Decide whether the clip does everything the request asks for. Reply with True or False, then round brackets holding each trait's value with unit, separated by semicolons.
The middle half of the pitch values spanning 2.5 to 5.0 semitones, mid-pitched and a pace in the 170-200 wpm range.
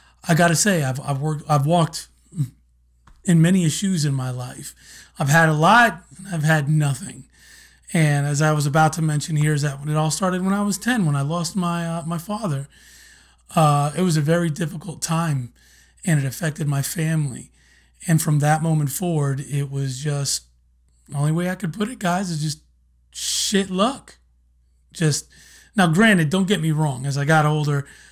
True (3.3 semitones; 155 Hz; 190 wpm)